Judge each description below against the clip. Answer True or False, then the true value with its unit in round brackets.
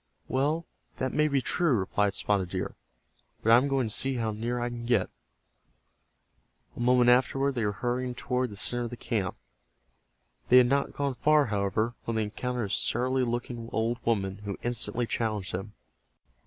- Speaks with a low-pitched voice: True (120 Hz)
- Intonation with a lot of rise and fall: False (3.2 semitones)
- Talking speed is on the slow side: False (180 wpm)